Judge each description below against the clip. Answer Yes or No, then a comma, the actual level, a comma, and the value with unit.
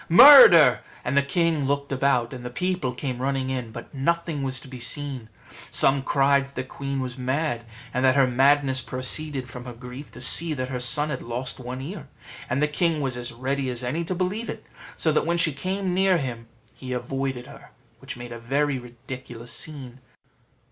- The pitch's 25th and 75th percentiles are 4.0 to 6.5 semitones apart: No, average, 3.0 semitones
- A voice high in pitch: No, low, 135 Hz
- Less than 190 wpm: No, average, 200 wpm